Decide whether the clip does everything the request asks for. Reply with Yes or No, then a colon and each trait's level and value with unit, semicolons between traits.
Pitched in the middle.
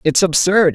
Yes: medium, 175 Hz